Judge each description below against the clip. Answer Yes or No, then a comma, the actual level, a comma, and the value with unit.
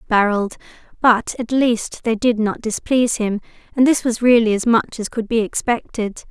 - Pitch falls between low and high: No, high, 230 Hz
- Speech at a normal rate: Yes, average, 180 wpm